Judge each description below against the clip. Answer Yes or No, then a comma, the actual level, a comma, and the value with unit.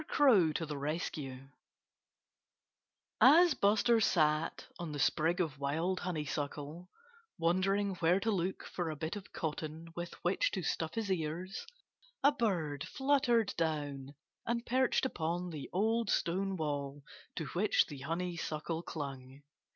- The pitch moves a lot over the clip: No, average, 4.6 semitones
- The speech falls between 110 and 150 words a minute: Yes, slow, 135 wpm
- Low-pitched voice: No, medium, 170 Hz